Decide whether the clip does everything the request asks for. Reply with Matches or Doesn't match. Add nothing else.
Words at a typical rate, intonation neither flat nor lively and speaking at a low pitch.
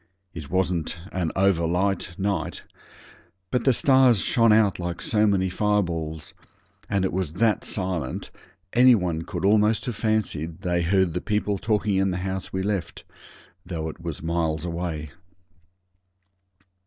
Matches